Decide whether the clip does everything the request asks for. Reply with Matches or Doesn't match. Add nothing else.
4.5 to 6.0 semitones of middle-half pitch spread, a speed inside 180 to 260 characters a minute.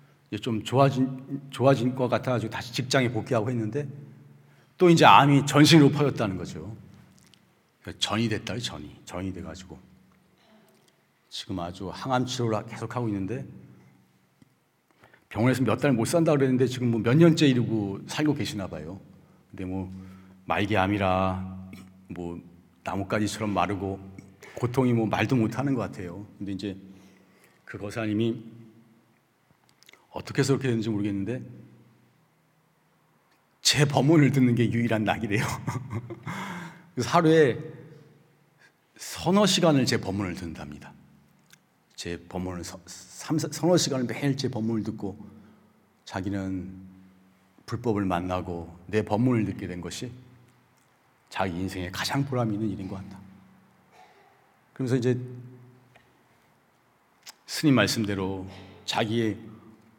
Matches